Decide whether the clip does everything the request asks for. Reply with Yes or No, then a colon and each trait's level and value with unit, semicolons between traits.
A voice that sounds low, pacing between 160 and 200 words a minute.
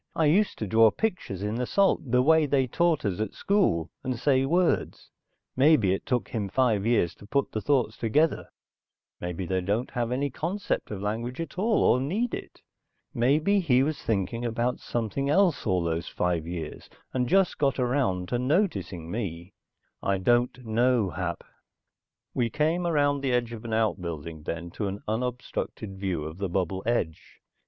Yes: low, 120 Hz; average, 175 wpm